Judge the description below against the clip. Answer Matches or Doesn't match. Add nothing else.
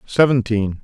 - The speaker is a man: Matches